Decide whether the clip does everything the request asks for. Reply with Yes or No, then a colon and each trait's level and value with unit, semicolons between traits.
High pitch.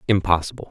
No: very low, 95 Hz